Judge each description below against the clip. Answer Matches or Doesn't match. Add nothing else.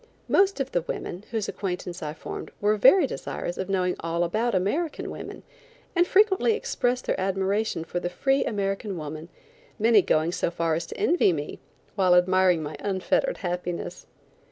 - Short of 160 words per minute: Doesn't match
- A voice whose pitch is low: Doesn't match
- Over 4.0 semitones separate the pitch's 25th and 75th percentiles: Matches